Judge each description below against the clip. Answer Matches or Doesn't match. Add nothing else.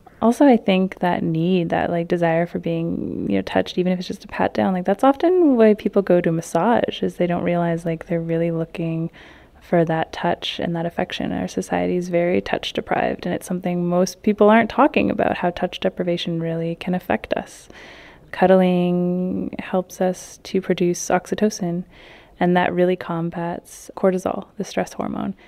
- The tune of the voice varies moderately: Doesn't match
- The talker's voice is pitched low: Doesn't match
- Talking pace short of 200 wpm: Matches